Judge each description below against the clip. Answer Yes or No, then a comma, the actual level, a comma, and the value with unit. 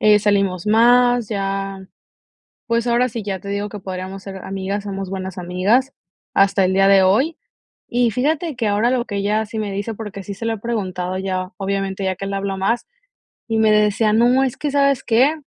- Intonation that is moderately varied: Yes, average, 3.2 semitones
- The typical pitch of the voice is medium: No, high, 205 Hz